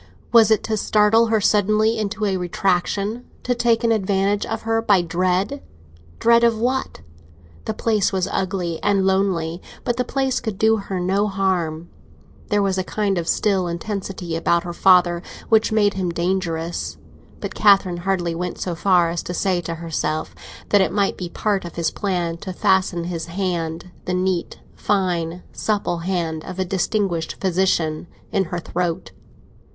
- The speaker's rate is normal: Yes, average, 160 wpm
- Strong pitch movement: No, average, 3.2 semitones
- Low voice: No, high, 190 Hz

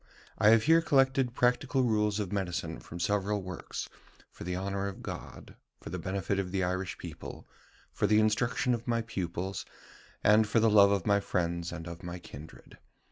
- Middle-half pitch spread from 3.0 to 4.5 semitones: Yes, average, 3.7 semitones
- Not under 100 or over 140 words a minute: No, average, 185 wpm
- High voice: No, low, 100 Hz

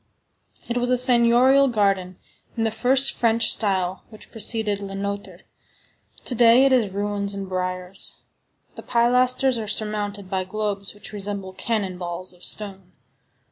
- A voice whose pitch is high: Yes, high, 205 Hz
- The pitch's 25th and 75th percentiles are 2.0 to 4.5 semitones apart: Yes, average, 3.4 semitones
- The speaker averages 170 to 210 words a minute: No, average, 145 wpm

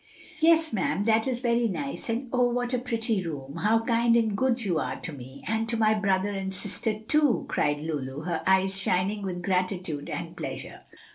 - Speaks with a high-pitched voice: Yes, high, 210 Hz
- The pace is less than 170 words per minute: No, average, 195 wpm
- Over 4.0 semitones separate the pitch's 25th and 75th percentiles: Yes, average, 4.4 semitones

